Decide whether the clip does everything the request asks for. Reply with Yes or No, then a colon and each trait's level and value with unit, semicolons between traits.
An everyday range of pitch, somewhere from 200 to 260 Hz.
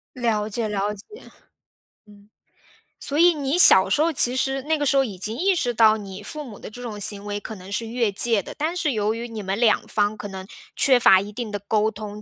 Yes: average, 4.2 semitones; high, 220 Hz